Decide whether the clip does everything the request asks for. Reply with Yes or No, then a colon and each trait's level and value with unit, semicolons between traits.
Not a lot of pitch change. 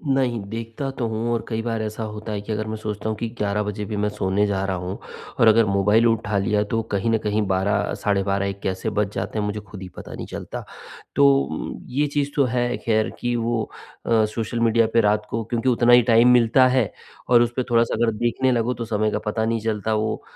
Yes: narrow, 2.1 semitones